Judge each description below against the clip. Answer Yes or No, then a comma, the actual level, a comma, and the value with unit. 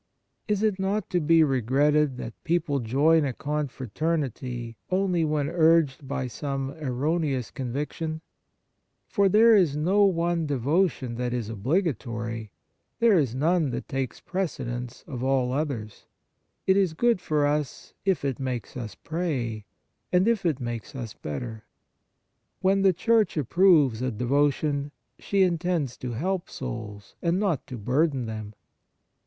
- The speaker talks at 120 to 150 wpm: Yes, average, 140 wpm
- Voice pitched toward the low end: No, medium, 145 Hz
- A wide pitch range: Yes, wide, 5.7 semitones